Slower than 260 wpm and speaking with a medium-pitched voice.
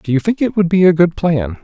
No: fast, 330 wpm; medium, 175 Hz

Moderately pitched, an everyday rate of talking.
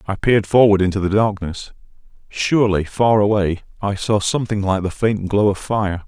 No: low, 100 Hz; average, 180 wpm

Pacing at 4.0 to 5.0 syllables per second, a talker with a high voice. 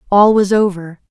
Yes: 4.9 syllables/s; high, 195 Hz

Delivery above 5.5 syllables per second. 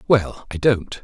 No: 4.1 syllables/s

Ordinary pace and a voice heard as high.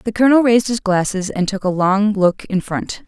No: fast, 235 wpm; high, 205 Hz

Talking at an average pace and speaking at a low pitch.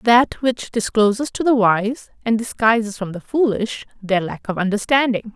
No: average, 170 wpm; high, 225 Hz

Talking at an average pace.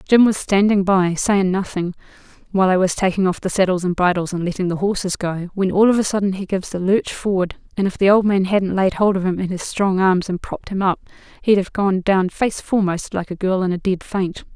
No: fast, 250 wpm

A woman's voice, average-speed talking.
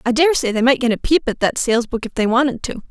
No: female; fast, 310 wpm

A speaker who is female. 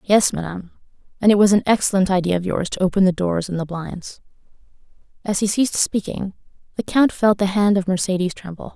Yes: female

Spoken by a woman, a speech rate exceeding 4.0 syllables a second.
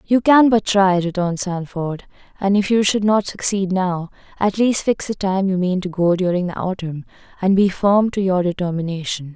Yes: female; 4.9 syllables/s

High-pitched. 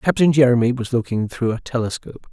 No: low, 125 Hz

